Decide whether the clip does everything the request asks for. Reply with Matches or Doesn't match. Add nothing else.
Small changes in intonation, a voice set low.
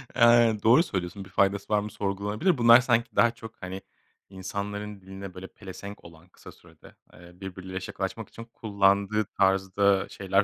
Matches